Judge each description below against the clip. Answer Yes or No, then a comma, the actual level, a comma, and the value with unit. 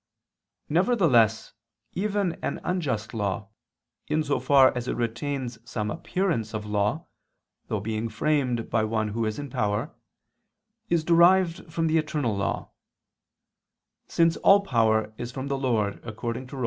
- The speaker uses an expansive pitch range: Yes, wide, 6.6 semitones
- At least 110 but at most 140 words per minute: No, average, 150 wpm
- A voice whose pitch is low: Yes, low, 125 Hz